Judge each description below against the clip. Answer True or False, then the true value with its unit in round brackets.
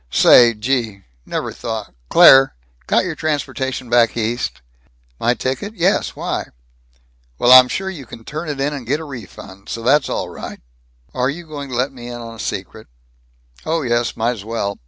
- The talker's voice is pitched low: True (125 Hz)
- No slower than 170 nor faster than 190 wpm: True (180 wpm)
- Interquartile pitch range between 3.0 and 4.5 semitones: True (3.9 semitones)